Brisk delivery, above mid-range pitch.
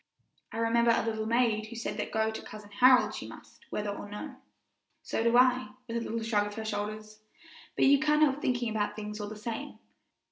Yes: fast, 215 wpm; high, 225 Hz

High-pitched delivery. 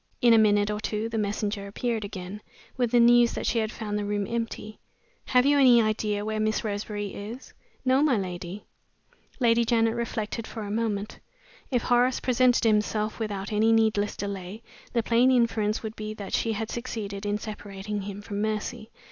Yes: high, 215 Hz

